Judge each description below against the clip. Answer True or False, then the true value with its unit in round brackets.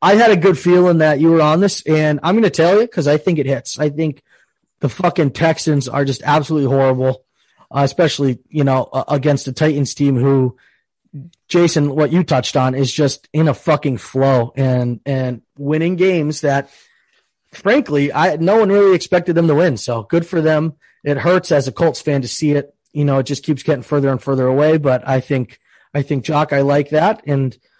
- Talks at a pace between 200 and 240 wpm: True (205 wpm)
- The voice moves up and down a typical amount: True (3.2 semitones)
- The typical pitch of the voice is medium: True (145 Hz)